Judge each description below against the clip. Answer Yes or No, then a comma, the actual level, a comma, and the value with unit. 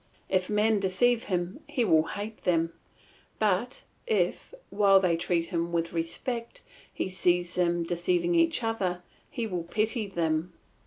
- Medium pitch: Yes, medium, 180 Hz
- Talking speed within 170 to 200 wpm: No, average, 145 wpm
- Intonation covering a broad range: No, average, 3.7 semitones